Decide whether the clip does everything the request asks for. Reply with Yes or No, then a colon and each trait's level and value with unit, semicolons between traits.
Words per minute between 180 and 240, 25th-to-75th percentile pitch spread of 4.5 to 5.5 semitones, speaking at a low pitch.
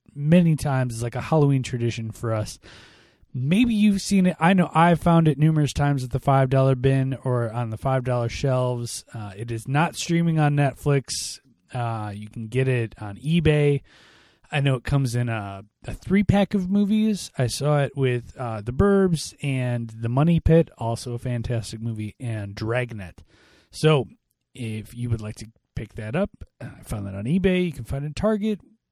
Yes: average, 190 wpm; average, 5.2 semitones; low, 130 Hz